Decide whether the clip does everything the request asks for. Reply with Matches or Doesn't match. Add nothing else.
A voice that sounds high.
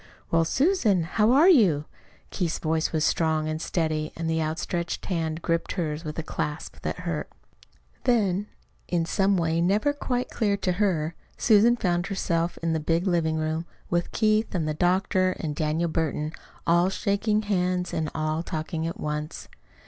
Doesn't match